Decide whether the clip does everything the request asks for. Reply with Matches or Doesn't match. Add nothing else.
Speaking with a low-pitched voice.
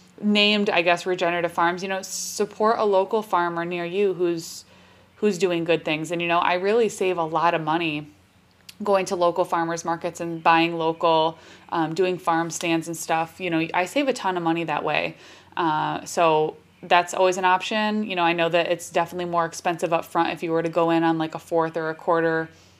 Doesn't match